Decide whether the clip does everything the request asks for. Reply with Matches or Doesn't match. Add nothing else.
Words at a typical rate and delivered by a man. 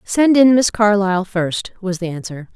Doesn't match